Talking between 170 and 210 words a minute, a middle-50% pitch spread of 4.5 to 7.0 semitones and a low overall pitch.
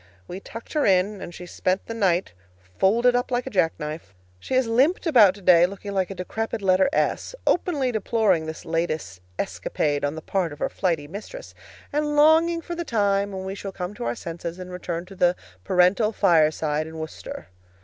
No: average, 190 wpm; average, 5.3 semitones; high, 190 Hz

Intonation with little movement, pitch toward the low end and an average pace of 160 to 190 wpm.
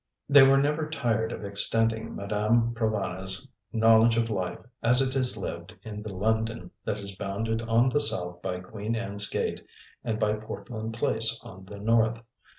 Yes: narrow, 2.3 semitones; low, 110 Hz; average, 165 wpm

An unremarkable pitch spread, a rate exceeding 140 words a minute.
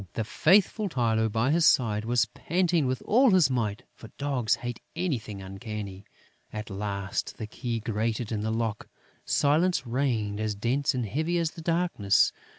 No: wide, 6.1 semitones; average, 160 wpm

